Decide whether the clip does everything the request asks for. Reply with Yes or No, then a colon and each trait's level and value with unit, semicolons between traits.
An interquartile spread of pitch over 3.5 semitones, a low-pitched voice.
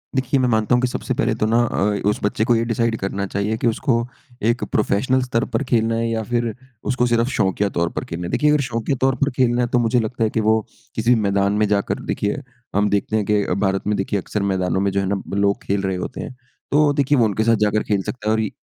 No: average, 3.2 semitones; low, 110 Hz